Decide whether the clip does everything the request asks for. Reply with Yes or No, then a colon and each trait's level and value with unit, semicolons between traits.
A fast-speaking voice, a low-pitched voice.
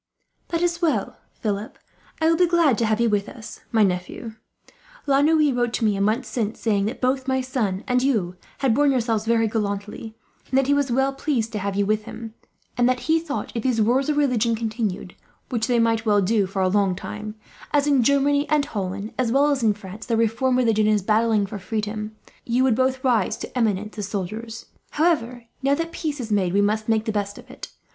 No: fast, 225 wpm; high, 230 Hz